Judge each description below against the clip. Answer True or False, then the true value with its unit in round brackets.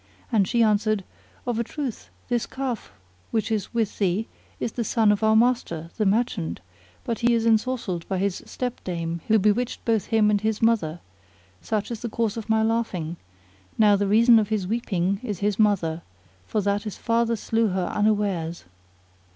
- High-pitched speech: True (215 Hz)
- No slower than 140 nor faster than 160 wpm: False (175 wpm)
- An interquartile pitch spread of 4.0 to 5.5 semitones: False (2.7 semitones)